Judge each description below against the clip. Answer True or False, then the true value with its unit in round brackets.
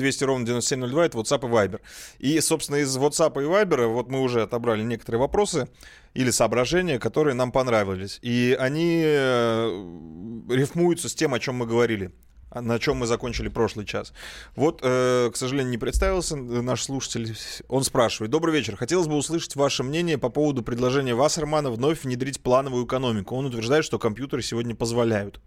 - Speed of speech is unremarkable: False (165 wpm)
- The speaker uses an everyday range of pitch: True (3.9 semitones)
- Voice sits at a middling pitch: False (125 Hz)